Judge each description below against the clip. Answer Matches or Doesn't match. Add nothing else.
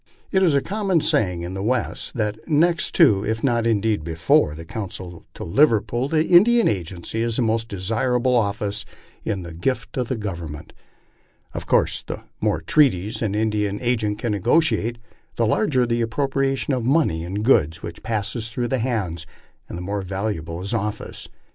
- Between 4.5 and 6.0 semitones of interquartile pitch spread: Matches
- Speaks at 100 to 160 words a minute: Doesn't match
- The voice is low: Matches